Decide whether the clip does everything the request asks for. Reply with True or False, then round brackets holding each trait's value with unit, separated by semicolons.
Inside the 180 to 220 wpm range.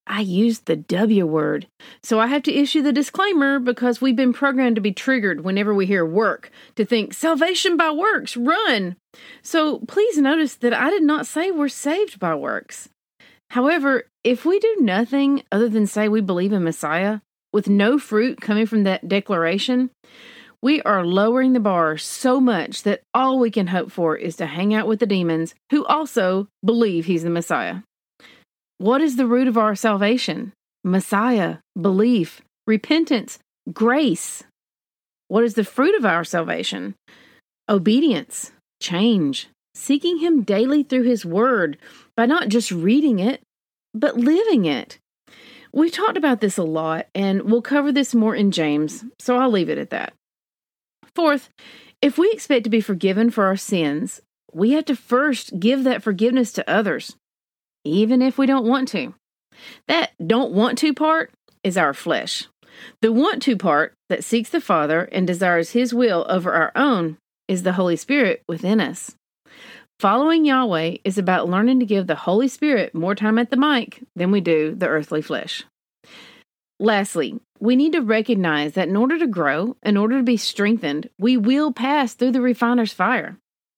False (170 wpm)